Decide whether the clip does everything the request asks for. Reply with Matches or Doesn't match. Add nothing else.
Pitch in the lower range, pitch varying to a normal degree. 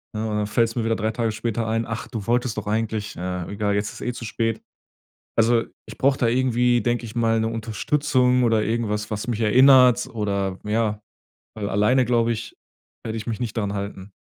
Doesn't match